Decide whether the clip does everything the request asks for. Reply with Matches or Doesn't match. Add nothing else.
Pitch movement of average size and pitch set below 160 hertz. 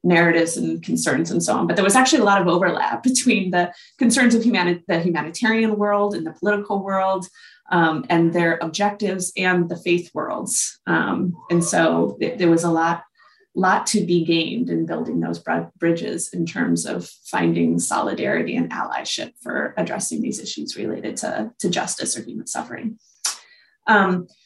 Doesn't match